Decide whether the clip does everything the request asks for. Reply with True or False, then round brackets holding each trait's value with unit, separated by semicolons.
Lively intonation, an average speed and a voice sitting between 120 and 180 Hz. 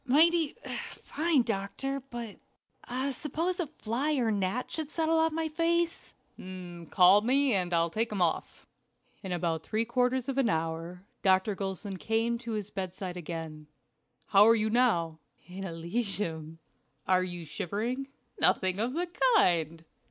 False (6.9 semitones; 145 wpm; 215 Hz)